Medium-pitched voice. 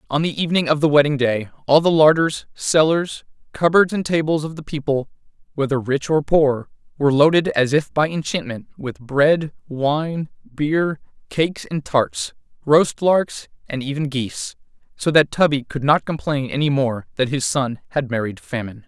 Yes: medium, 145 Hz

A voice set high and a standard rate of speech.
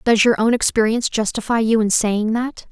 No: high, 225 Hz; fast, 220 wpm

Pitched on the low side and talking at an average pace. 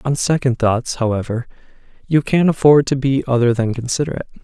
Yes: low, 130 Hz; average, 160 wpm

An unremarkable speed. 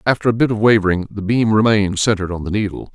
No: fast, 245 wpm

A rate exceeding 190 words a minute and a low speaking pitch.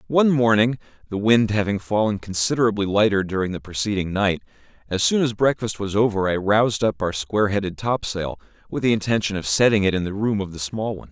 Yes: fast, 205 wpm; low, 105 Hz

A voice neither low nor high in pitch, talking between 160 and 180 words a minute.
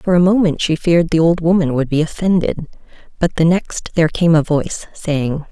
No: medium, 165 Hz; fast, 205 wpm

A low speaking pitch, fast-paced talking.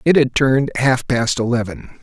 No: low, 125 Hz; average, 180 wpm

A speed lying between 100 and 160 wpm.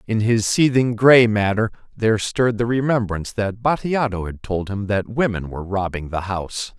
No: average, 175 wpm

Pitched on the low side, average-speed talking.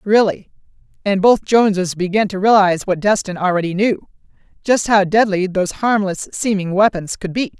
No: high, 195 Hz; average, 150 wpm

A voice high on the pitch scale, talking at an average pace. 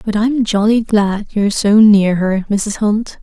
Yes: high, 210 Hz; average, 185 wpm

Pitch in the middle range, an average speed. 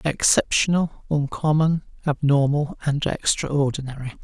No: medium, 145 Hz; slow, 70 wpm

